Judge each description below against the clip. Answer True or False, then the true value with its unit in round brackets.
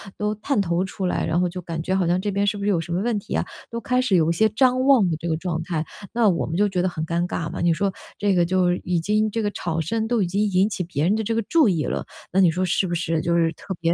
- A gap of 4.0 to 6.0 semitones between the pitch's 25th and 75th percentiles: False (3.6 semitones)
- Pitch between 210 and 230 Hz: False (185 Hz)